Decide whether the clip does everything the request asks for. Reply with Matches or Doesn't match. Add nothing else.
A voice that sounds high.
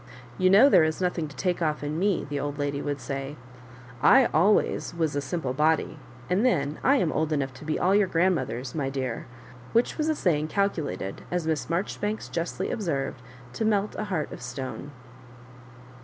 Doesn't match